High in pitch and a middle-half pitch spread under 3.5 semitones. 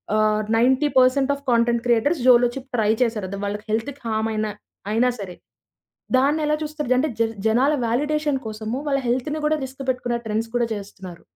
No: high, 245 Hz; average, 4.2 semitones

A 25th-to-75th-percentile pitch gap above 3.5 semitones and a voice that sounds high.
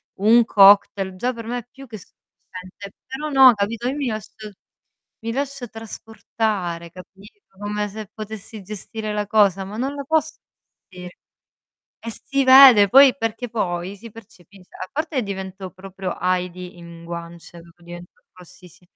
Yes: average, 4.1 semitones; high, 210 Hz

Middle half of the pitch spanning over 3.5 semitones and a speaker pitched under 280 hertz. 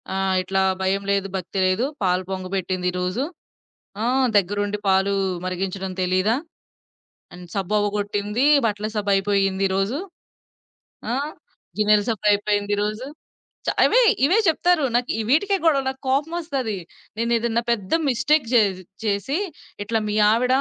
Yes: average, 4.1 semitones; high, 205 Hz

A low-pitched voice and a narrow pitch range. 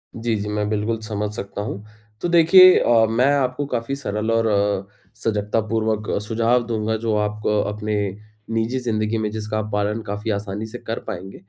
Yes: low, 110 Hz; narrow, 1.7 semitones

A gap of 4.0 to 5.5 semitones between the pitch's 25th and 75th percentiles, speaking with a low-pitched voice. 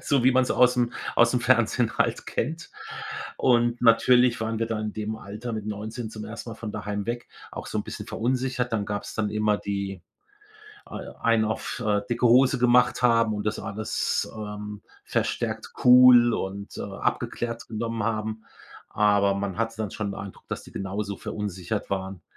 No: narrow, 2.6 semitones; low, 110 Hz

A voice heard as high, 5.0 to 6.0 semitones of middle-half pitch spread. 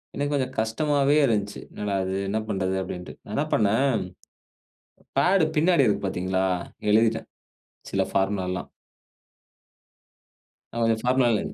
No: low, 110 Hz; wide, 5.6 semitones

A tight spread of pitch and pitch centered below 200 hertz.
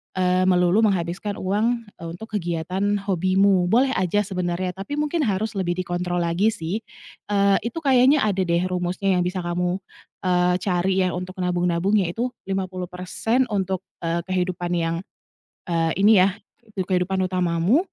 Yes: narrow, 2.2 semitones; medium, 185 Hz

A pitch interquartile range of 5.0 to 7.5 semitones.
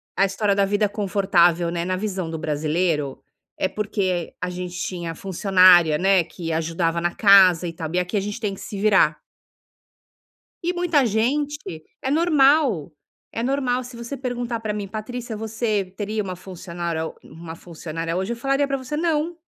Yes: wide, 5.5 semitones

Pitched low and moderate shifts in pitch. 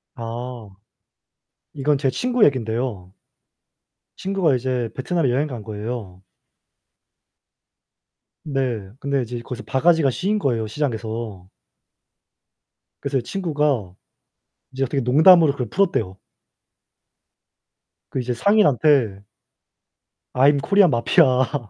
Yes: low, 130 Hz; average, 4.3 semitones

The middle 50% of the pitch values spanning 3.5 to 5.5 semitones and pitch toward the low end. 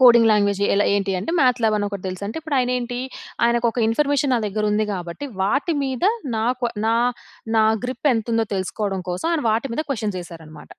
No: average, 3.9 semitones; high, 225 Hz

